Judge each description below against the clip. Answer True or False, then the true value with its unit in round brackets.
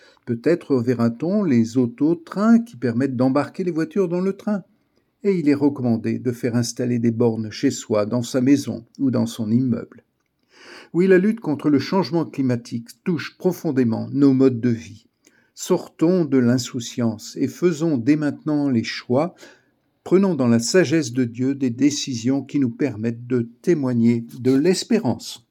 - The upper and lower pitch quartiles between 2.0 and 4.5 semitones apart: False (5.6 semitones)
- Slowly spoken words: False (160 wpm)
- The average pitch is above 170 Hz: False (135 Hz)